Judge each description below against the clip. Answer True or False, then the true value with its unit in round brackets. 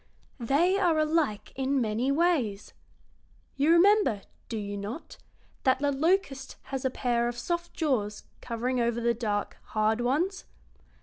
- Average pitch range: False (5.7 semitones)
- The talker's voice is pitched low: False (260 Hz)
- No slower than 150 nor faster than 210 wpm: False (140 wpm)